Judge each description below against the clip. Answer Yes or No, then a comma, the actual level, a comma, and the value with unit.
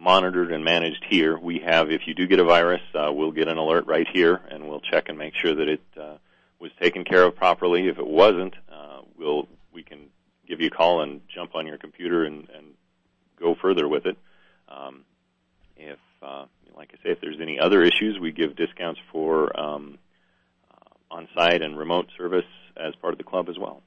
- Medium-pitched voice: No, very low, 80 Hz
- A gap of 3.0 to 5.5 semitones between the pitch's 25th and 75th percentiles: No, narrow, 2.4 semitones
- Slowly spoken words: No, fast, 205 wpm